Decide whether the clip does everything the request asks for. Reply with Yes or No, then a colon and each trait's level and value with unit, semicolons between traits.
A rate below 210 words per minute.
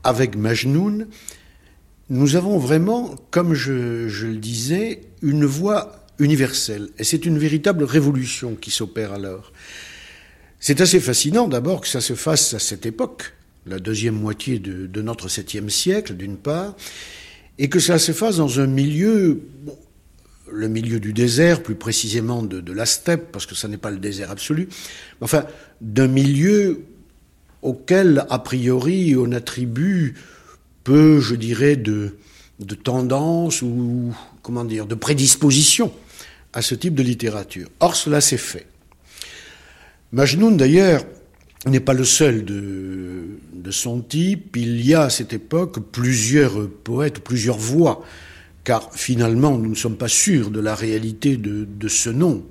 Yes: average, 150 wpm